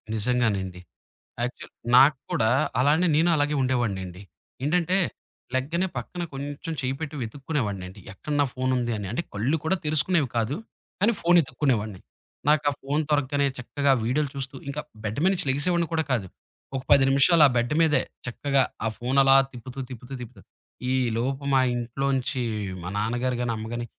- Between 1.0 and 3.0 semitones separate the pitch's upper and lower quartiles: No, average, 3.9 semitones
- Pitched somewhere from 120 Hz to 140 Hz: Yes, low, 135 Hz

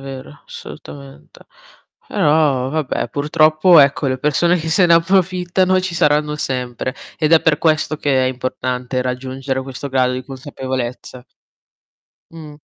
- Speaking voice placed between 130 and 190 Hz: Yes, medium, 140 Hz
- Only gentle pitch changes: No, average, 3.6 semitones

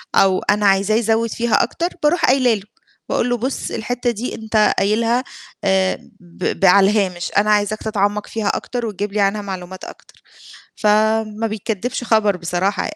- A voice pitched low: No, high, 210 Hz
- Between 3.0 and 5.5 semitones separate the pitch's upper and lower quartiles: No, narrow, 2.5 semitones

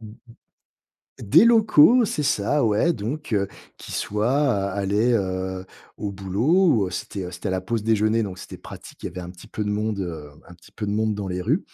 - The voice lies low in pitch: Yes, low, 105 Hz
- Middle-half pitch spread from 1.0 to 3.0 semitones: No, average, 3.8 semitones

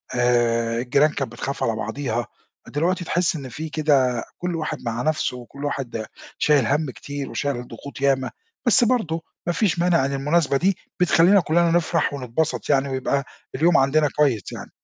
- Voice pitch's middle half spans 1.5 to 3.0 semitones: No, average, 4.5 semitones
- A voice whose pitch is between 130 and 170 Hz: Yes, medium, 140 Hz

